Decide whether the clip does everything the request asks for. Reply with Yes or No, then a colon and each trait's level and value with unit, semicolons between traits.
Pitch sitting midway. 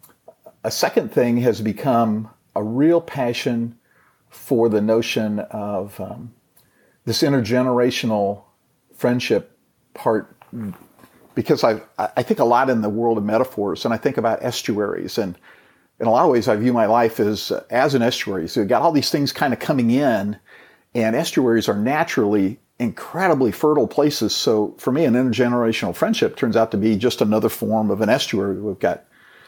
No: low, 115 Hz